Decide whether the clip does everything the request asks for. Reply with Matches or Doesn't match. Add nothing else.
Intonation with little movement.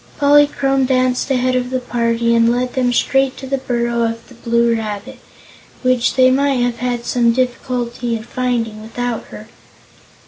Matches